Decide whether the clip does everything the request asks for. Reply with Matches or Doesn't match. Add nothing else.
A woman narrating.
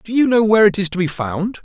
Doesn't match